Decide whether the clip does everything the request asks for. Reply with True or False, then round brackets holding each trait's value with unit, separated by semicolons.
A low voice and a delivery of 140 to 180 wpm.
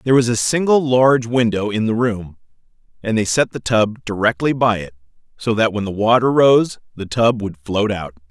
False (110 Hz; 200 wpm)